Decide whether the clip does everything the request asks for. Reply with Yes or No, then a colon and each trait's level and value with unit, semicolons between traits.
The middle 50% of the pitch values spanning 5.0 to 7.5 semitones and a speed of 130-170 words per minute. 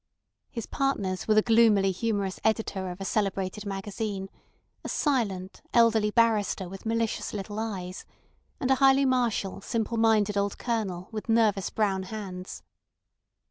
No: average, 2.8 semitones; average, 140 wpm